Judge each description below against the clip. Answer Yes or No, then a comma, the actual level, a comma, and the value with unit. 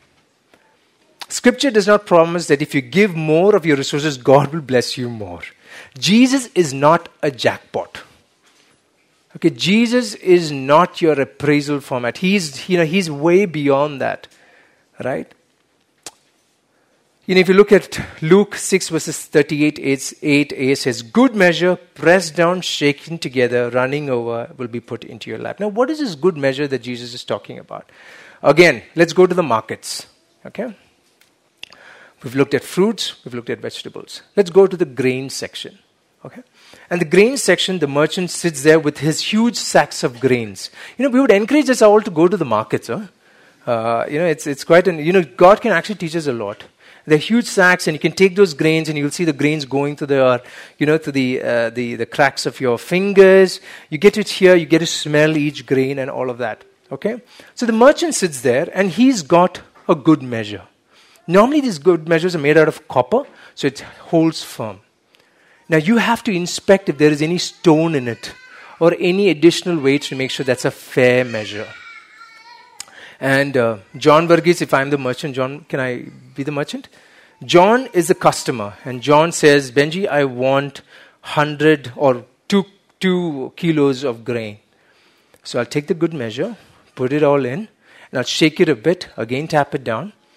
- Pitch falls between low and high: Yes, medium, 160 Hz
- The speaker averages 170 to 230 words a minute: Yes, average, 190 wpm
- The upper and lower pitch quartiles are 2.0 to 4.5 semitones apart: No, wide, 5.4 semitones